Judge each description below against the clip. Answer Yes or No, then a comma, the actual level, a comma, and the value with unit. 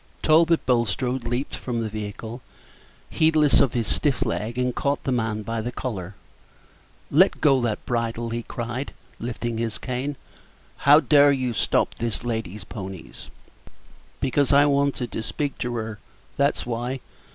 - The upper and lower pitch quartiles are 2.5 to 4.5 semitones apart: Yes, average, 3.5 semitones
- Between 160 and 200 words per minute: No, average, 150 wpm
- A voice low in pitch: Yes, low, 120 Hz